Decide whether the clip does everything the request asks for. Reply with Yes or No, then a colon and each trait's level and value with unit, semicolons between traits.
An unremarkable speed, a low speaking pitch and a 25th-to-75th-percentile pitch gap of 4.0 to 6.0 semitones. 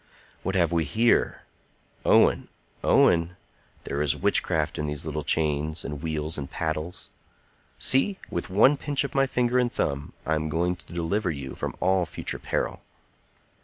Yes: average, 160 wpm; very low, 85 Hz; average, 4.4 semitones